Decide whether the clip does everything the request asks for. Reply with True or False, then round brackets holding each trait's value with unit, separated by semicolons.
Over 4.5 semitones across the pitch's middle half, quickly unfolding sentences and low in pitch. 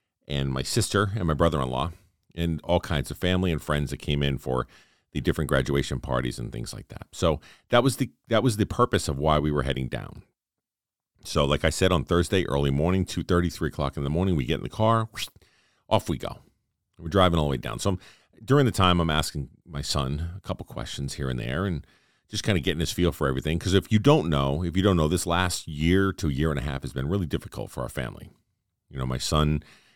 True (5.1 semitones; 240 wpm; 85 Hz)